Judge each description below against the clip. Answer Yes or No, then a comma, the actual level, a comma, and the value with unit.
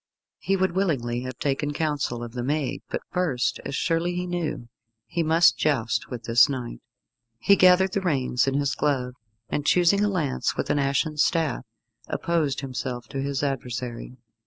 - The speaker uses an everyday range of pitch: Yes, average, 5.0 semitones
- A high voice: No, medium, 140 Hz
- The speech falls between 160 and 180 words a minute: Yes, average, 170 wpm